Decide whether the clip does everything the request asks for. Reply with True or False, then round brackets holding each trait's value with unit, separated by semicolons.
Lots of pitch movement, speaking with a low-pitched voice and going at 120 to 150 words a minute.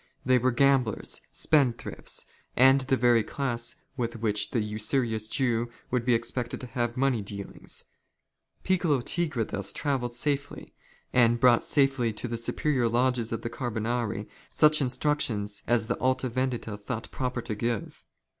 False (2.5 semitones; 120 Hz; 145 wpm)